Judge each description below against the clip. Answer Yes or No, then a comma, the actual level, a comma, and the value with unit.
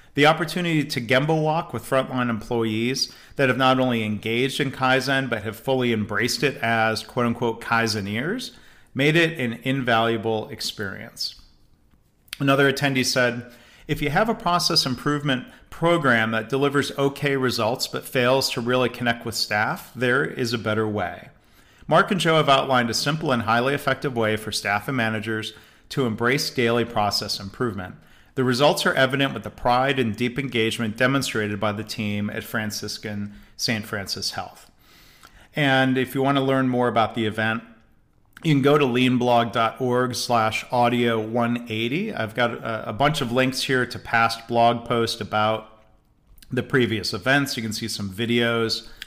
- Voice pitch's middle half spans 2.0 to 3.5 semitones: Yes, average, 3.2 semitones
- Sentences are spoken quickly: No, average, 160 wpm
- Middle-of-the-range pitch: No, low, 120 Hz